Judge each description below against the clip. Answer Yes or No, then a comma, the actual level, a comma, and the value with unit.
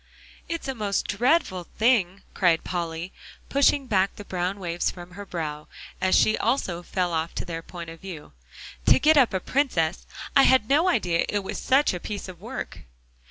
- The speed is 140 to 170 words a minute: No, average, 185 wpm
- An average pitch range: No, wide, 6.1 semitones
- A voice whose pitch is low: No, high, 190 Hz